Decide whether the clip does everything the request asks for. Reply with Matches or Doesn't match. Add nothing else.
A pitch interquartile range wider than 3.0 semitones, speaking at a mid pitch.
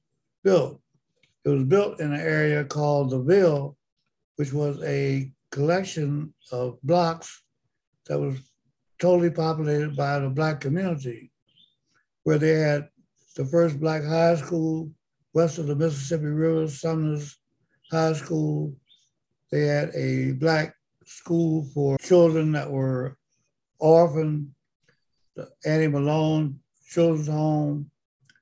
Doesn't match